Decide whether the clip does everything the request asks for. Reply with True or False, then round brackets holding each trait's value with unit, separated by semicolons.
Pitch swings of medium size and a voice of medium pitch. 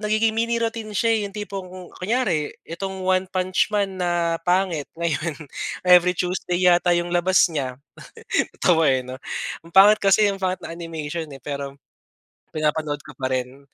True (3.9 semitones; 180 Hz)